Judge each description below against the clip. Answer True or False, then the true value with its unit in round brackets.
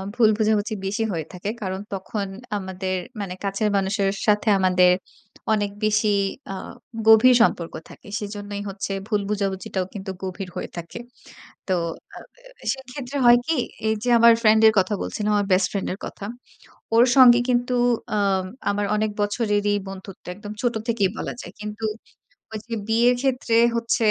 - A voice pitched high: True (205 Hz)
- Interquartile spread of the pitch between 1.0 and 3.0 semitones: True (2.6 semitones)